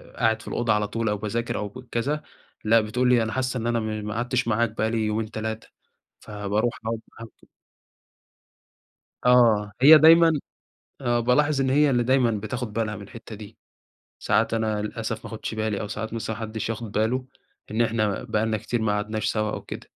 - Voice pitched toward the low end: Yes, low, 110 Hz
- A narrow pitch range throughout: Yes, narrow, 2.0 semitones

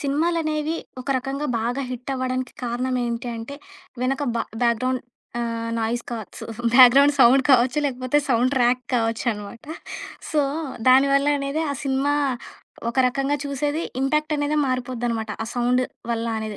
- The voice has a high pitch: Yes, very high, 255 Hz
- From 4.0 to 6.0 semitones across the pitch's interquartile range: No, average, 2.9 semitones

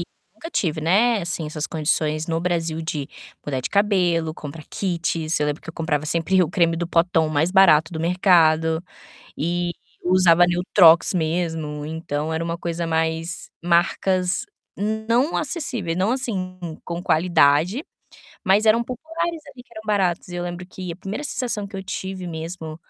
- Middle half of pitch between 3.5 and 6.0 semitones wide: No, average, 3.0 semitones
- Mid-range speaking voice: Yes, medium, 175 Hz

